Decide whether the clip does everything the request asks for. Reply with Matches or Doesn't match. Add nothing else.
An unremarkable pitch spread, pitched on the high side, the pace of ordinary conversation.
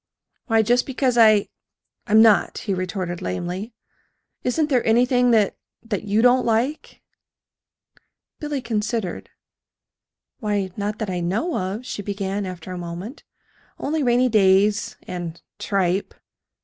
Doesn't match